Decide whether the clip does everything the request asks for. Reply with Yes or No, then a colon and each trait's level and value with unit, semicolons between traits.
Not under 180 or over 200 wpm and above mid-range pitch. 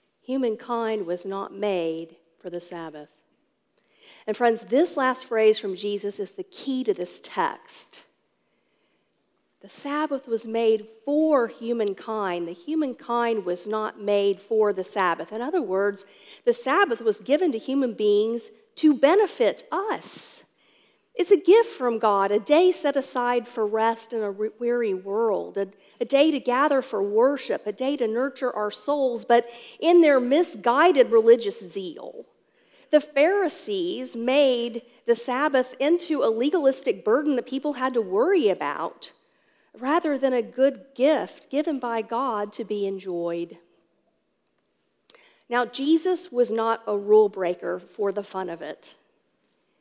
No: average, 140 wpm; high, 245 Hz